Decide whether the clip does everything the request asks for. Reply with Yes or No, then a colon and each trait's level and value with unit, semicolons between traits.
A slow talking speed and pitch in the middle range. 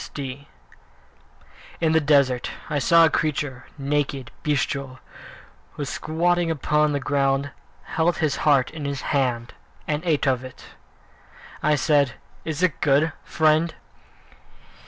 Yes: slow, 125 wpm; medium, 145 Hz